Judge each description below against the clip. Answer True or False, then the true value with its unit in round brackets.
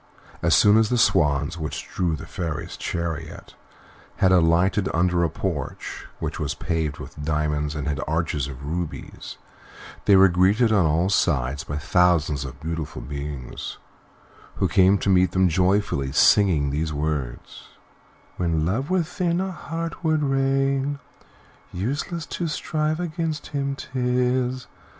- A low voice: True (90 Hz)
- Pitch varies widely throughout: True (8.8 semitones)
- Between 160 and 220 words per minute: False (140 wpm)